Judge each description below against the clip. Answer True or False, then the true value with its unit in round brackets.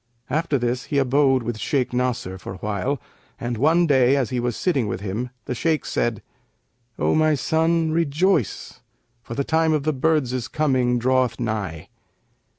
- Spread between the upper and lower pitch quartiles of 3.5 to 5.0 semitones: True (4.5 semitones)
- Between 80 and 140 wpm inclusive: False (165 wpm)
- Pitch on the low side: True (130 Hz)